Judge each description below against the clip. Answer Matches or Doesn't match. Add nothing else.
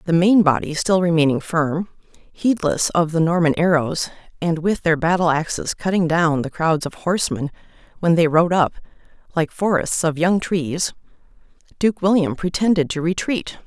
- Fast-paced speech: Doesn't match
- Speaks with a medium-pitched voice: Matches